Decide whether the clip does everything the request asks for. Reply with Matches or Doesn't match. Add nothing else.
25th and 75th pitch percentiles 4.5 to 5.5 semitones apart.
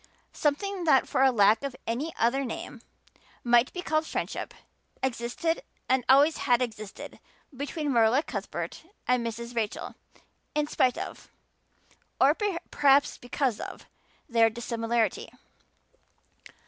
Doesn't match